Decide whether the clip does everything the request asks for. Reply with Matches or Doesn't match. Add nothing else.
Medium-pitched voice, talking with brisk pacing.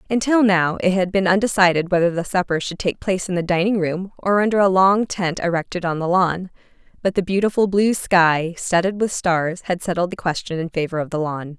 Matches